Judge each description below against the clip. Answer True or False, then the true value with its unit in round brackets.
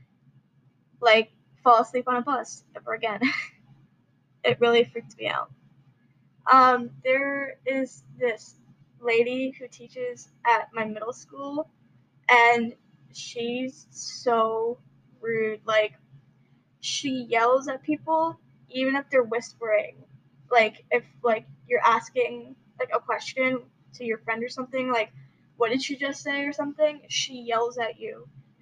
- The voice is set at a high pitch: True (235 Hz)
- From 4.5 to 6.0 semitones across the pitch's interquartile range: False (3.4 semitones)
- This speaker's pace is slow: True (130 wpm)